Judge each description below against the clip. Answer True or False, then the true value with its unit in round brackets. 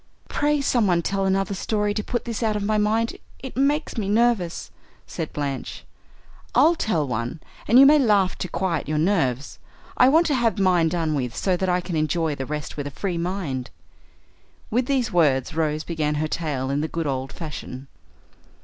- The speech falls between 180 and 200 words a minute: True (190 wpm)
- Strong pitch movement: True (6.3 semitones)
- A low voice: False (180 Hz)